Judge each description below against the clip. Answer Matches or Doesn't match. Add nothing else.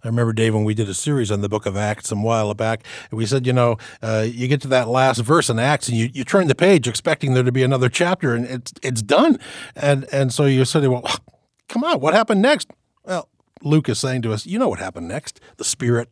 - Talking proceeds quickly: Matches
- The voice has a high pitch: Doesn't match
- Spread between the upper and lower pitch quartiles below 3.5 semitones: Doesn't match